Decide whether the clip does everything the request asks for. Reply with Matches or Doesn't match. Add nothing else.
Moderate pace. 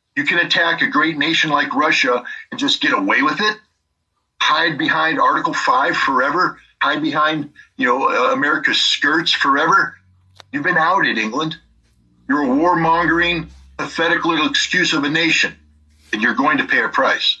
Matches